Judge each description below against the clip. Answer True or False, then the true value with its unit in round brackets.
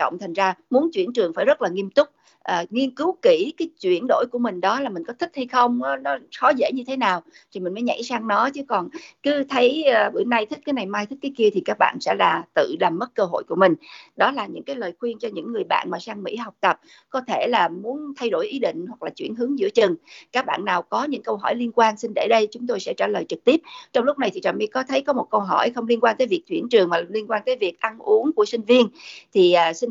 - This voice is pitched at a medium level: False (250 Hz)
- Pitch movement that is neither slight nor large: False (6.0 semitones)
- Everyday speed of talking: False (295 wpm)